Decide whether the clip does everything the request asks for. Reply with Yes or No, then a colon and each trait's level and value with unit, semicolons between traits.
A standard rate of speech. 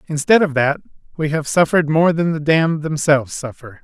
Yes: average, 190 wpm